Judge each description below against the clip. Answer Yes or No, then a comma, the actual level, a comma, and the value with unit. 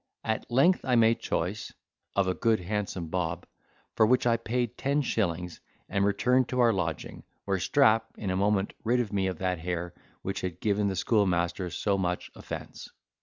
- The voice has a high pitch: No, low, 100 Hz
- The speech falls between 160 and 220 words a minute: Yes, average, 175 wpm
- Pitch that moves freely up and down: No, average, 4.3 semitones